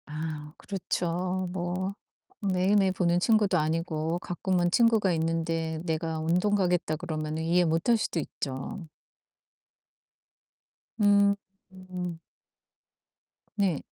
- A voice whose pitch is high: No, medium, 175 Hz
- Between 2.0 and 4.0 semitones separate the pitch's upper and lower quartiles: Yes, average, 2.8 semitones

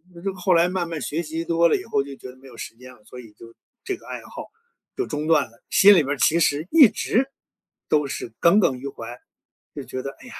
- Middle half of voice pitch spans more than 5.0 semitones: Yes, wide, 5.4 semitones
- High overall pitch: No, medium, 155 Hz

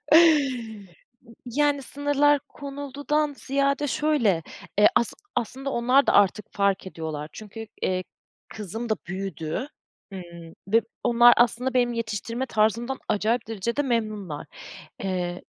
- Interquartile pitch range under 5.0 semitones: No, wide, 5.6 semitones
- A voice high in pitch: Yes, high, 230 Hz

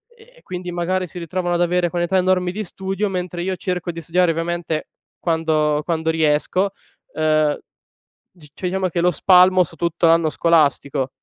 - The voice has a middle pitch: Yes, medium, 175 Hz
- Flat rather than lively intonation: Yes, narrow, 2.1 semitones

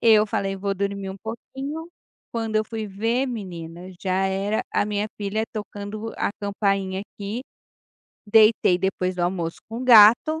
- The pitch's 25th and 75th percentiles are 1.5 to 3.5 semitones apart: Yes, narrow, 2.5 semitones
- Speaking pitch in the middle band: No, high, 205 Hz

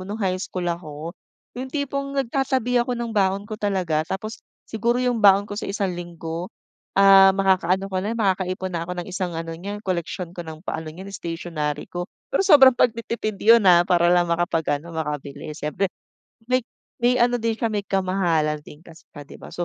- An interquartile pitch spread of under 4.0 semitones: No, average, 4.7 semitones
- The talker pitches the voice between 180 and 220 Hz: Yes, high, 190 Hz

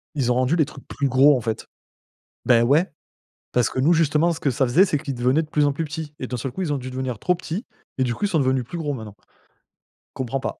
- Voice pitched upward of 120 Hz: Yes, low, 135 Hz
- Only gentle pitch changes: No, average, 3.6 semitones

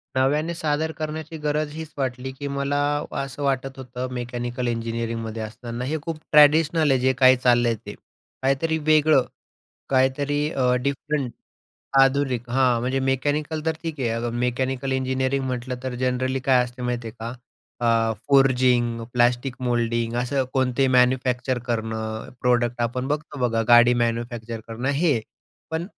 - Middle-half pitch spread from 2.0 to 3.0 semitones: Yes, narrow, 2.6 semitones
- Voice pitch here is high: No, low, 130 Hz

